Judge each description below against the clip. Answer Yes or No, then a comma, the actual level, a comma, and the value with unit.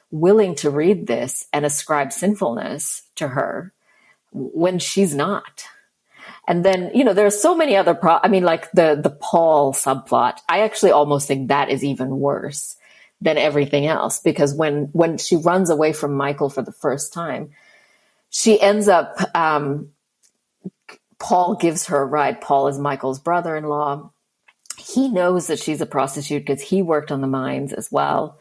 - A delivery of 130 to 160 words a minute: No, average, 170 wpm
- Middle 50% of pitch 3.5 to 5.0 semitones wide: Yes, average, 4.1 semitones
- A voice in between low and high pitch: Yes, medium, 155 Hz